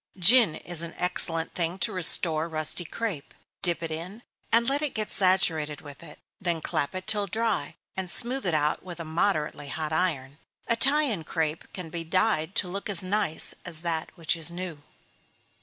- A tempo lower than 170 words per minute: No, average, 180 wpm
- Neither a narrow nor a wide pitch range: Yes, average, 3.9 semitones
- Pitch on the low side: No, medium, 175 Hz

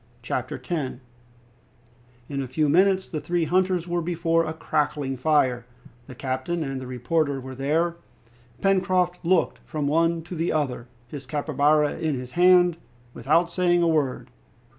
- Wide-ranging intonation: No, average, 4.2 semitones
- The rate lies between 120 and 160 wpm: Yes, average, 150 wpm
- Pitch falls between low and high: Yes, medium, 155 Hz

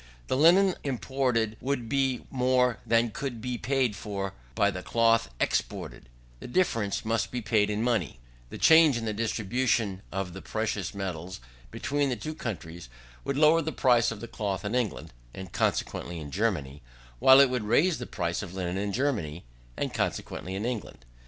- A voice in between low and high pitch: No, low, 115 Hz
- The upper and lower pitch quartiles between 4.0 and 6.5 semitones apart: Yes, average, 5.0 semitones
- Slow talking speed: No, average, 170 wpm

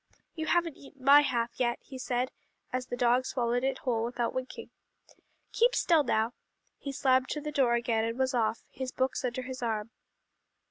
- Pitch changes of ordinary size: No, narrow, 2.1 semitones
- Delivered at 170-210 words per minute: Yes, average, 185 wpm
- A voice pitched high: Yes, very high, 255 Hz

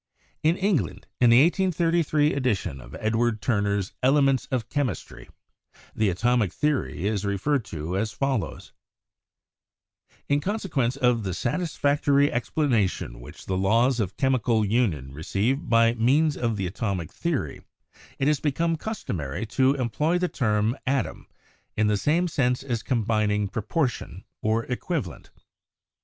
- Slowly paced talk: Yes, slow, 130 wpm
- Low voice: Yes, low, 120 Hz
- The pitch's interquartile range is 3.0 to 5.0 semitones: No, wide, 5.6 semitones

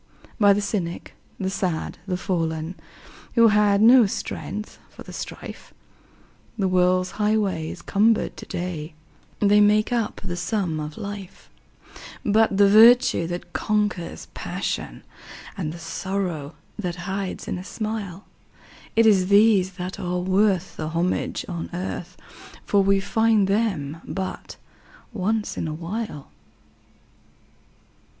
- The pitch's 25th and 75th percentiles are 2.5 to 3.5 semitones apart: Yes, average, 3.0 semitones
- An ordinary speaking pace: No, slow, 130 wpm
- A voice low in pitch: No, high, 195 Hz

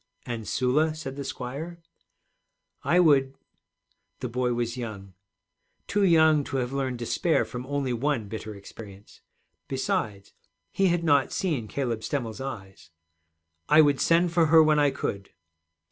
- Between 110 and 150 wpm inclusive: Yes, average, 145 wpm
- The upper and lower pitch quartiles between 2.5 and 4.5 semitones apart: No, average, 5.0 semitones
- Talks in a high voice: No, low, 135 Hz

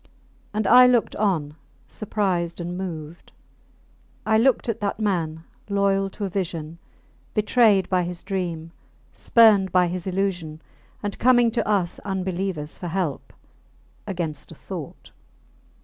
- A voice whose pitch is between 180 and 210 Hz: Yes, high, 190 Hz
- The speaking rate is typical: No, slow, 130 wpm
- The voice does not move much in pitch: No, average, 3.3 semitones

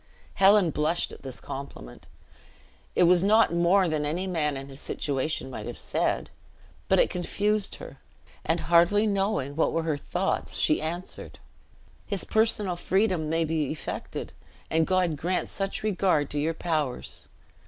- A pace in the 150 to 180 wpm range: Yes, average, 155 wpm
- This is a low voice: No, medium, 170 Hz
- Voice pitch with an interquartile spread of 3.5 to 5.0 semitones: Yes, average, 4.1 semitones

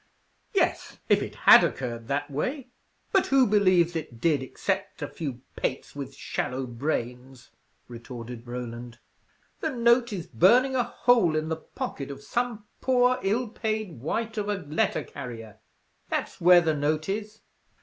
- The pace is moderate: Yes, average, 150 wpm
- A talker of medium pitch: Yes, medium, 160 Hz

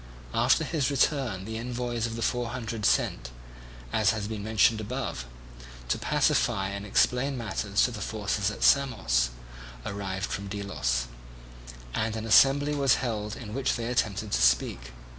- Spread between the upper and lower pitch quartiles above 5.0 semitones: No, average, 3.7 semitones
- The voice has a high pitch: No, low, 110 Hz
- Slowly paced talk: No, average, 155 wpm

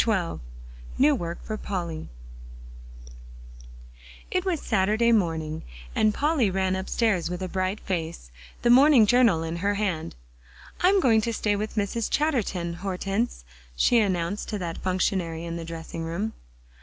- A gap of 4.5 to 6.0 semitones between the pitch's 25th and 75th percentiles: Yes, average, 4.9 semitones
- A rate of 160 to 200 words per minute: No, average, 145 wpm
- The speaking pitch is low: No, high, 195 Hz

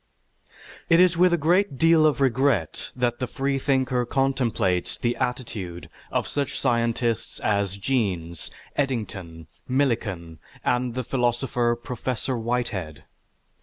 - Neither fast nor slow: No, slow, 115 wpm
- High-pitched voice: No, low, 125 Hz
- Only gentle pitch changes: No, average, 4.8 semitones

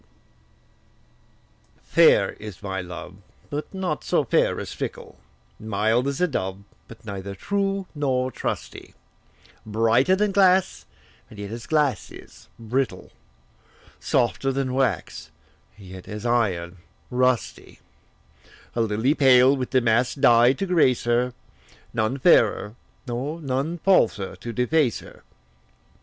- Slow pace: Yes, slow, 125 wpm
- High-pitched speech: No, low, 125 Hz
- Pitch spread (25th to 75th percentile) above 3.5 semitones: Yes, average, 4.5 semitones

